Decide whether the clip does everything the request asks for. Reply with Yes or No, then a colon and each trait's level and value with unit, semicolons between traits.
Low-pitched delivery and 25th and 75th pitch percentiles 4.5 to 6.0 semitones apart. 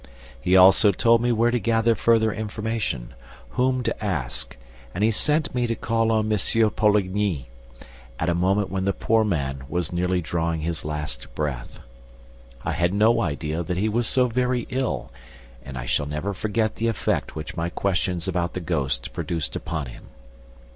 Yes: very low, 95 Hz; wide, 5.5 semitones